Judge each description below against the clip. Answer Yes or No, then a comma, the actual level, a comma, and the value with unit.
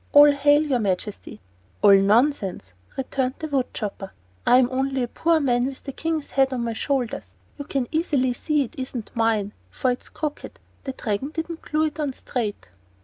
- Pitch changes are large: No, average, 4.3 semitones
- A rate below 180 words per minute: No, average, 185 wpm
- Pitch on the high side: Yes, very high, 260 Hz